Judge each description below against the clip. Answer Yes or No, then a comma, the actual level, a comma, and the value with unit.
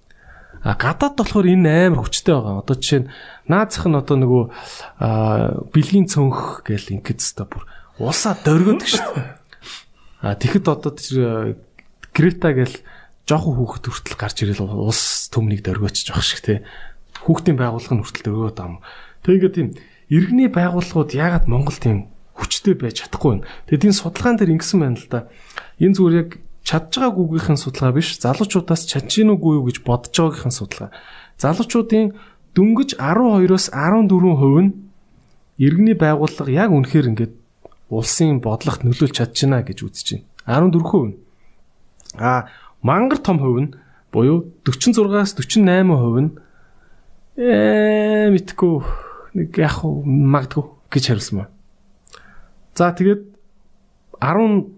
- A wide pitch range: Yes, wide, 7.4 semitones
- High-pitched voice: No, medium, 150 Hz